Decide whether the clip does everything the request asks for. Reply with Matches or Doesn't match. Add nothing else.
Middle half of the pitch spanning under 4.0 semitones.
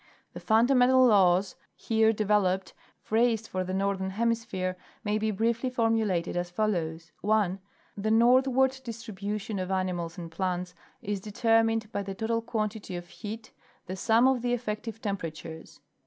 Matches